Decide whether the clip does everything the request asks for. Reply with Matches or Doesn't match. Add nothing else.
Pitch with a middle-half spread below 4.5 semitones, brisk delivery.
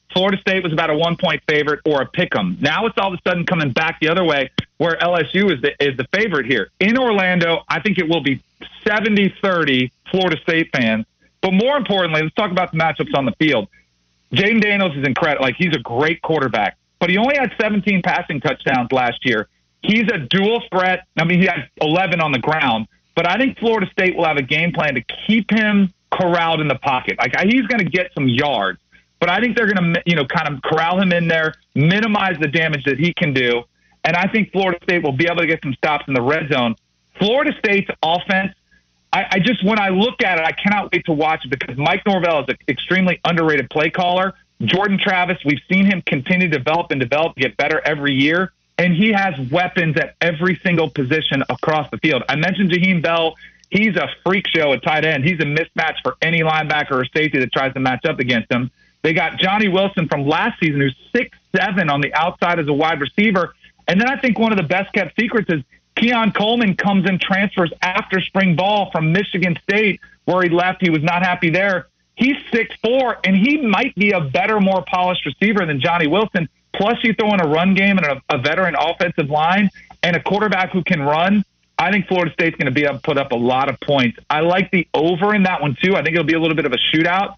Matches